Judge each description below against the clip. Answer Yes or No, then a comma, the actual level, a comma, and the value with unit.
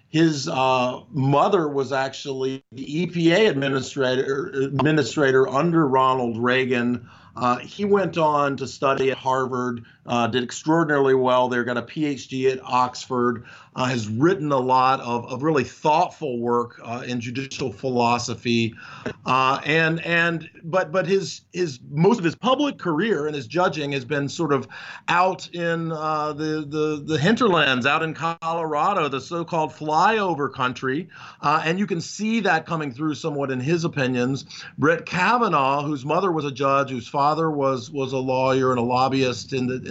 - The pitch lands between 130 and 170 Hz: Yes, medium, 140 Hz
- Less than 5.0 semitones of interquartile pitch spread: Yes, average, 3.8 semitones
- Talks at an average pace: Yes, average, 160 wpm